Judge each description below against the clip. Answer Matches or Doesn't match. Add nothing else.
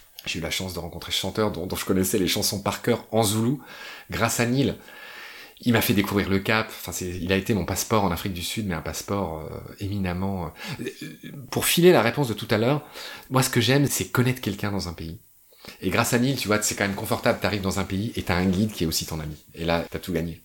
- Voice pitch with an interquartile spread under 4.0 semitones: Doesn't match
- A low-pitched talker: Matches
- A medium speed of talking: Doesn't match